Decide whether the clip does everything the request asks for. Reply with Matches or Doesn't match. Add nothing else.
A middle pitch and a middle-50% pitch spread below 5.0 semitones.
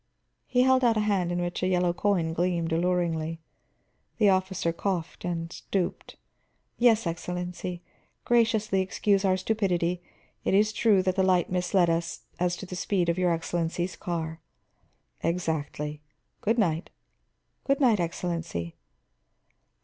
Matches